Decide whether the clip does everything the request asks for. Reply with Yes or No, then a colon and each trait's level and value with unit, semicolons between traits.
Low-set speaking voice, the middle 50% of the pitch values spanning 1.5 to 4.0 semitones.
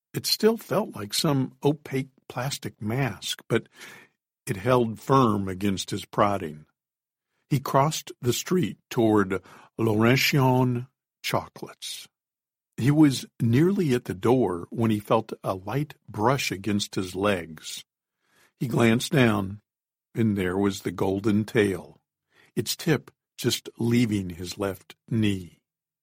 No: low, 115 Hz; average, 4.8 semitones